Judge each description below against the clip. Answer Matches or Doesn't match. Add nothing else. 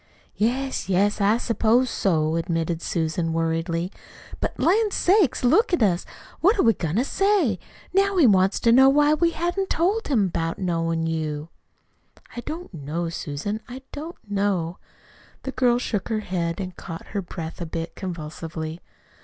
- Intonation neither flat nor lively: Doesn't match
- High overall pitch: Matches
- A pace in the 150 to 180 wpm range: Matches